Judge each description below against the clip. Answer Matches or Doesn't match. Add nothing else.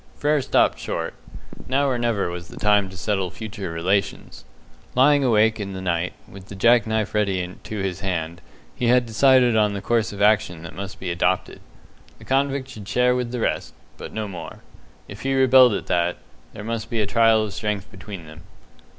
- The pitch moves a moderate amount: Matches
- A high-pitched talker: Doesn't match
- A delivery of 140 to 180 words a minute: Doesn't match